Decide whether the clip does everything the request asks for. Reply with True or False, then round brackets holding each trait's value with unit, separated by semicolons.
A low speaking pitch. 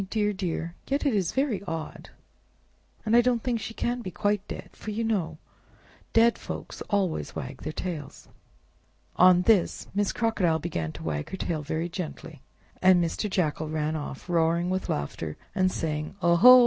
False (180 Hz)